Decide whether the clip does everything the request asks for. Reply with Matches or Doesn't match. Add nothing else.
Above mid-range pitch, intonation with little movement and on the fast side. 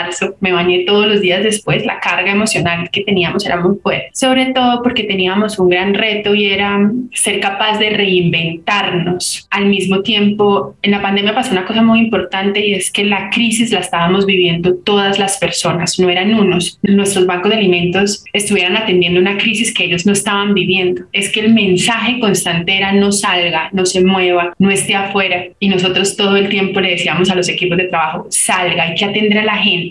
Matches